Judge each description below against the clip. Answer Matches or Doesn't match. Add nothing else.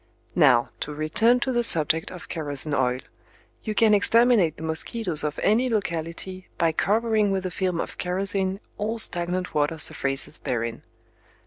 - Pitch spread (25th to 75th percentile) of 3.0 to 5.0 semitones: Doesn't match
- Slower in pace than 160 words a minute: Matches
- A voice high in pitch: Doesn't match